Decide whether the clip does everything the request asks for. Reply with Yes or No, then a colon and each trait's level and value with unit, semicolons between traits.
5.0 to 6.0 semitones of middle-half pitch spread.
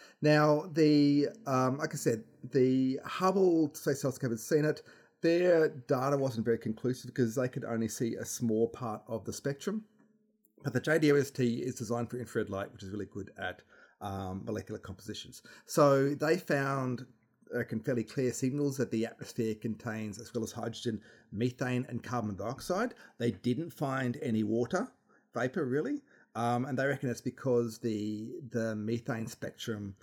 No: average, 4.0 semitones